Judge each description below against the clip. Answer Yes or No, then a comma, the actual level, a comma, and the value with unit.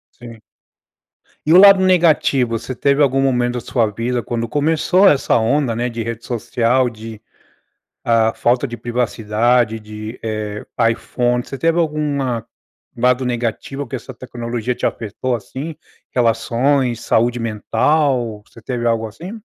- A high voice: No, low, 120 Hz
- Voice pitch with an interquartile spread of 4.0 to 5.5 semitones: No, average, 3.0 semitones